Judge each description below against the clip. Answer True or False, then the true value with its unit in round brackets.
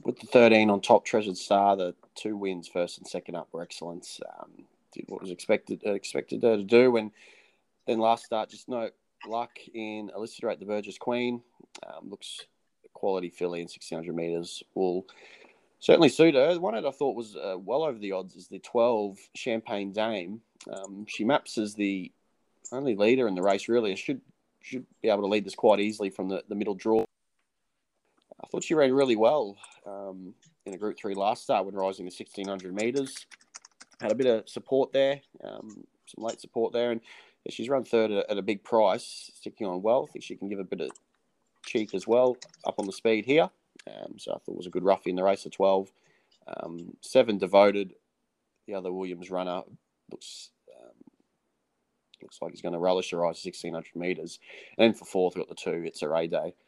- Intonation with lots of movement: False (3.5 semitones)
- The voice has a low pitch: True (100 Hz)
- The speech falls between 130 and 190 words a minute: False (205 wpm)